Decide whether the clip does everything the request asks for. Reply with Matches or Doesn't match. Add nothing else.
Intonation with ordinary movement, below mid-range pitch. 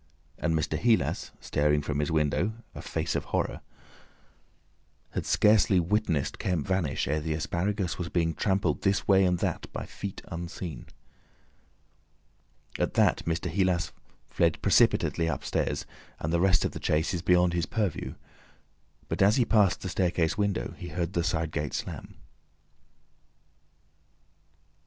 Matches